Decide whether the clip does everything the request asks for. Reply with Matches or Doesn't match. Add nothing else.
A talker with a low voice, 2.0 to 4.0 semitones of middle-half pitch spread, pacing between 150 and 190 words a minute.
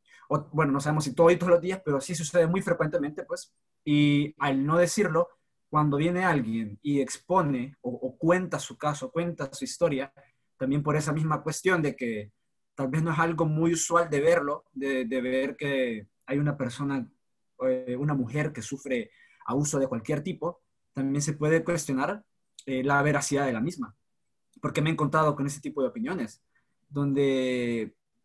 Doesn't match